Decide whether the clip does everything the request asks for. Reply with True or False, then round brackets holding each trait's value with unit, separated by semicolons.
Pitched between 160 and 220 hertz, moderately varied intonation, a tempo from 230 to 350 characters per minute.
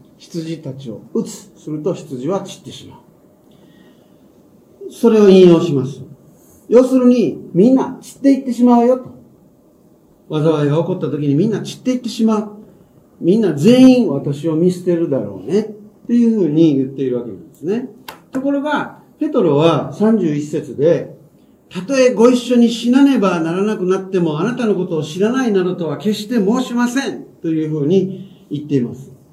False (190 Hz; 6.9 semitones; 330 characters per minute)